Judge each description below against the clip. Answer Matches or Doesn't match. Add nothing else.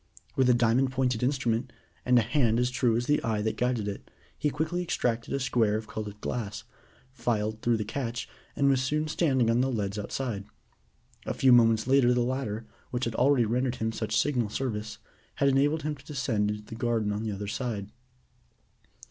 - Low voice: Matches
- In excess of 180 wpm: Matches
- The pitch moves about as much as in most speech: Matches